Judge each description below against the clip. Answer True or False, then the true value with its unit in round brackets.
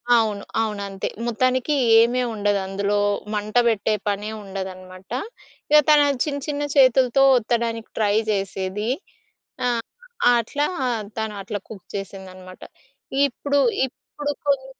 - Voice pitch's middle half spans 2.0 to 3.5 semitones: False (4.4 semitones)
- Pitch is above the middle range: True (215 Hz)